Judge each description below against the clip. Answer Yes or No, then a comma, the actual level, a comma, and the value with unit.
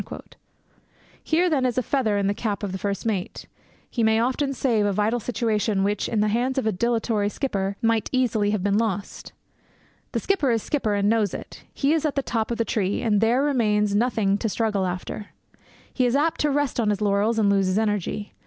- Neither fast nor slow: No, fast, 215 wpm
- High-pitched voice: Yes, high, 220 Hz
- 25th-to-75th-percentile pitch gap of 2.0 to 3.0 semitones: No, average, 3.4 semitones